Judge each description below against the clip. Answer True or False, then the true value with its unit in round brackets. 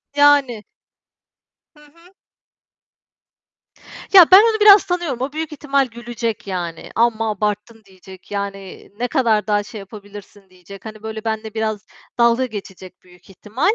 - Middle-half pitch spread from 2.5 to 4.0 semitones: False (5.3 semitones)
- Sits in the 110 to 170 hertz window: False (220 Hz)